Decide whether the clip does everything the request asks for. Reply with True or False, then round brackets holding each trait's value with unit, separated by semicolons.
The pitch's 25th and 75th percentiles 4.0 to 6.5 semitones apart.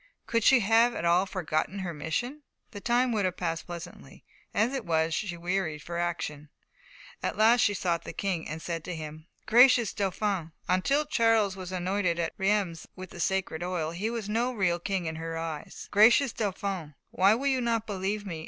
True (4.5 semitones)